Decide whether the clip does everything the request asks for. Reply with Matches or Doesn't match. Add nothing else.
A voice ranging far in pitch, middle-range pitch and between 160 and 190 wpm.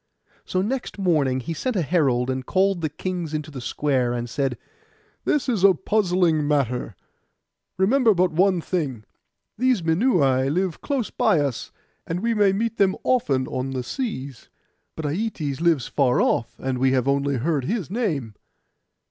Matches